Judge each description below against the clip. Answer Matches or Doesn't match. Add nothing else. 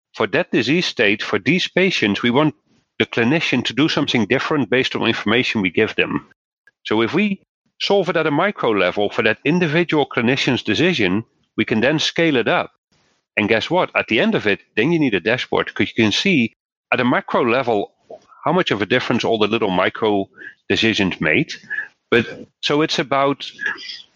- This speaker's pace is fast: Doesn't match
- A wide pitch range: Matches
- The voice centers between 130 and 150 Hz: Matches